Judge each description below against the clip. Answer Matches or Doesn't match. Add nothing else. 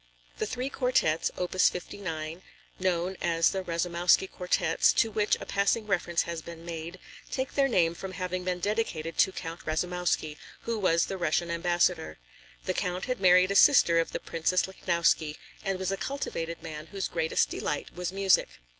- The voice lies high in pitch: Doesn't match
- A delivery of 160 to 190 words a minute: Matches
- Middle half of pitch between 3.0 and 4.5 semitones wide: Doesn't match